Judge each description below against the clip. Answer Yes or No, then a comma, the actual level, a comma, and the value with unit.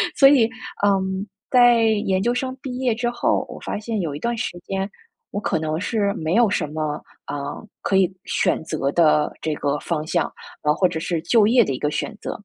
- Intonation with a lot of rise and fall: Yes, wide, 7.0 semitones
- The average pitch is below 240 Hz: Yes, high, 195 Hz